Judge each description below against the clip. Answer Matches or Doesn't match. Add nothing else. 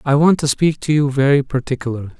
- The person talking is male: Matches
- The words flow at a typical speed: Doesn't match